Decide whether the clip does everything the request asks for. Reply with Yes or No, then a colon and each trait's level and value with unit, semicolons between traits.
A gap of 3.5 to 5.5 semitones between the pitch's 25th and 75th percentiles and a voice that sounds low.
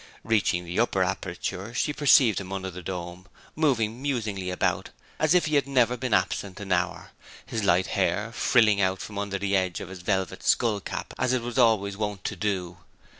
Yes: average, 4.0 semitones; low, 100 Hz